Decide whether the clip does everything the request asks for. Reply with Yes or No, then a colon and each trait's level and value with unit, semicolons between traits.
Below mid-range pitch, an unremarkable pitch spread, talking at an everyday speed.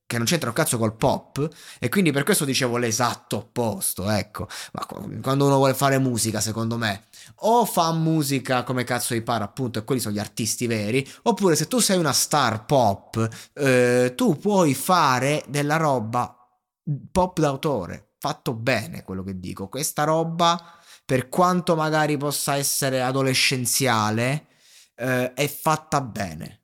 Yes: low, 130 Hz; average, 4.6 semitones; average, 155 wpm